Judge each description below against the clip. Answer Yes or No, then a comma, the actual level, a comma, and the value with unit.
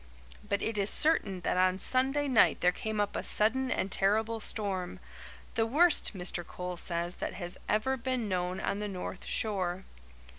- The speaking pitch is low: No, high, 205 Hz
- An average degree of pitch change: Yes, average, 3.9 semitones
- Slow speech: No, average, 175 wpm